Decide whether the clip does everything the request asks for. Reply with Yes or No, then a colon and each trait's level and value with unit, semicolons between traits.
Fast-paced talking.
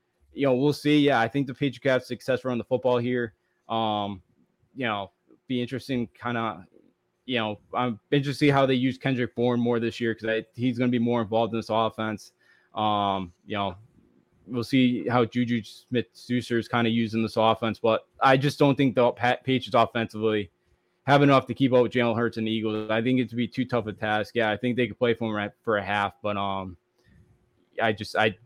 Yes: fast, 220 wpm